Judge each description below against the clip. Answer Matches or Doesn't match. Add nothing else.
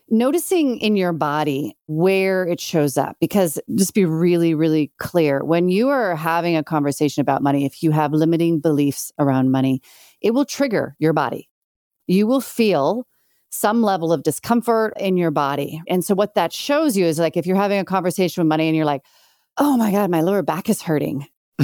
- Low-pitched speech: Doesn't match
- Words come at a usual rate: Matches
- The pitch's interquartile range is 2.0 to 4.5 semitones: Doesn't match